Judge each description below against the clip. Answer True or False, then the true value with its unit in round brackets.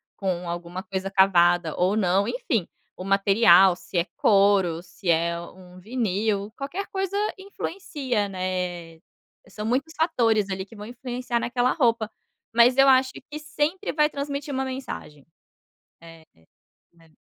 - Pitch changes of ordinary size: False (6.2 semitones)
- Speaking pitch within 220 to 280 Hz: False (205 Hz)